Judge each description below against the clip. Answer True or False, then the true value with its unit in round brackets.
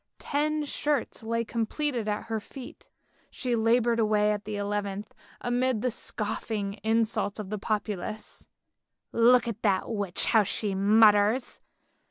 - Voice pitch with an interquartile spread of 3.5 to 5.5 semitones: False (2.4 semitones)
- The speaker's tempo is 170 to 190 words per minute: False (140 wpm)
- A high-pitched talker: True (220 Hz)